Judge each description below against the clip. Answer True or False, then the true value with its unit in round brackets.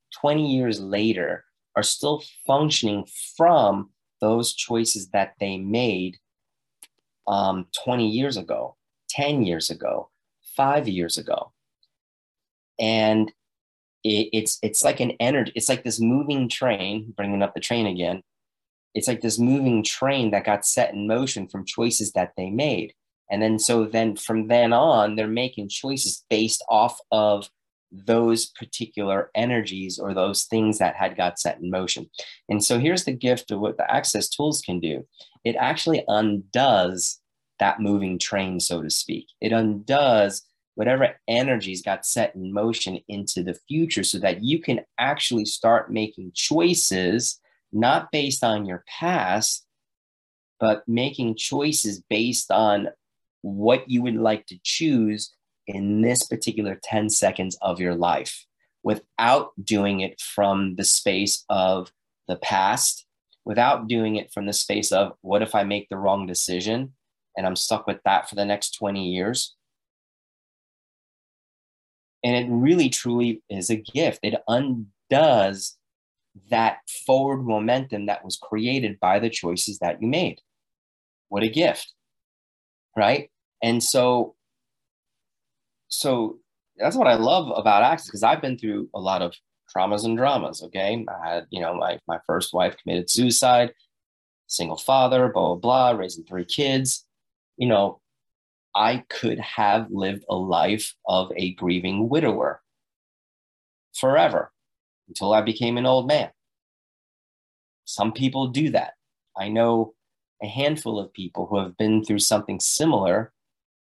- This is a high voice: False (110 Hz)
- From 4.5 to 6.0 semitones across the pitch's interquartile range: False (3.6 semitones)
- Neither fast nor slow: True (145 wpm)